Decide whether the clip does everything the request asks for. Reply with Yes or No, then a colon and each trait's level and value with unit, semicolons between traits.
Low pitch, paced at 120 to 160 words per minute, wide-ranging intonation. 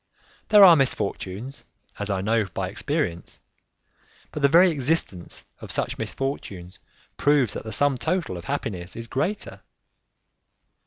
Yes: low, 125 Hz; slow, 135 wpm; wide, 7.2 semitones